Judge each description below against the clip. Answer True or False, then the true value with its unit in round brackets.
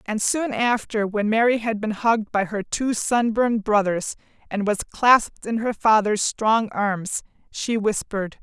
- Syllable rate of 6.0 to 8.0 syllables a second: False (4.4 syllables/s)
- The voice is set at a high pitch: True (215 Hz)